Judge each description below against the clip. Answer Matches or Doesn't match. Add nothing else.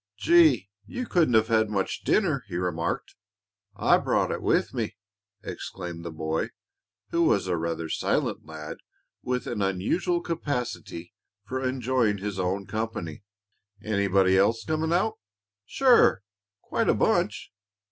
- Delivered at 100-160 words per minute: Matches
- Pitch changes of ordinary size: Doesn't match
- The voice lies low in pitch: Matches